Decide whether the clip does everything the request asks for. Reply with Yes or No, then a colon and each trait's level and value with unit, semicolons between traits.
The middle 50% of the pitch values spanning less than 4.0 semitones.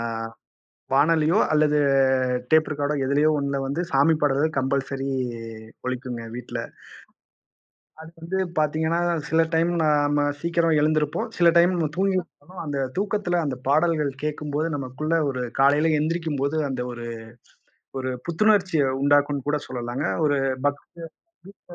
Yes: average, 2.9 semitones